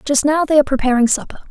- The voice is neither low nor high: No, very high, 280 Hz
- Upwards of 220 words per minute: Yes, fast, 240 wpm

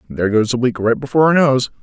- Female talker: No, male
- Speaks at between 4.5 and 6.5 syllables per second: No, 7.0 syllables/s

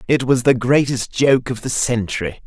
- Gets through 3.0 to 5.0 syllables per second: Yes, 4.8 syllables/s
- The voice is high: No, low, 125 Hz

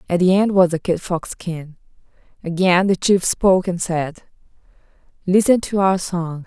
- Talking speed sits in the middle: Yes, average, 165 wpm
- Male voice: No, female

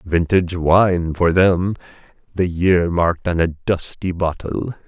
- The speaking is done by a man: Yes, male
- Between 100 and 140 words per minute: Yes, slow, 135 wpm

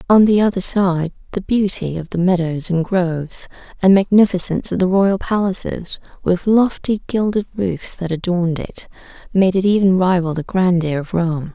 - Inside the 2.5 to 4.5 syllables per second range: No, 4.9 syllables/s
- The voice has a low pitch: No, medium, 185 Hz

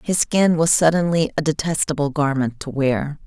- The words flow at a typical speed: Yes, average, 165 wpm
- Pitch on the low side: No, medium, 155 Hz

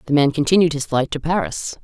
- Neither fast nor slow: No, fast, 230 wpm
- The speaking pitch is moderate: Yes, medium, 145 Hz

